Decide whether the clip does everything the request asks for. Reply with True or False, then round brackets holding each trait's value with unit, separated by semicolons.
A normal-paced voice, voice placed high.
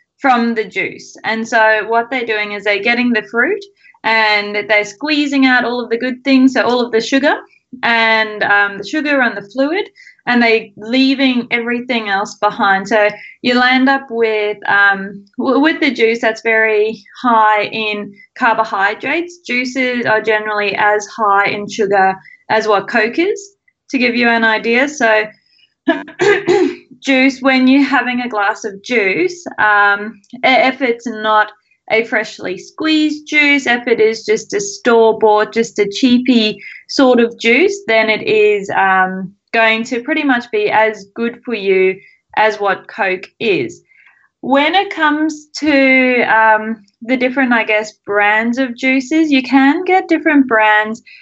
True (155 wpm; 235 Hz)